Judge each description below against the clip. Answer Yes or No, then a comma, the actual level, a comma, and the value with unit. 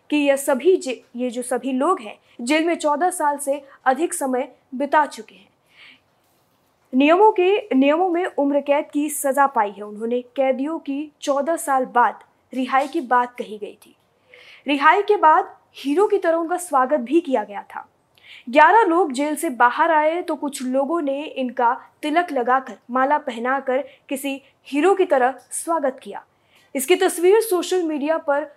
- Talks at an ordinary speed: Yes, average, 165 wpm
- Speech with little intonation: No, average, 3.7 semitones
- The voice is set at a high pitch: Yes, very high, 285 Hz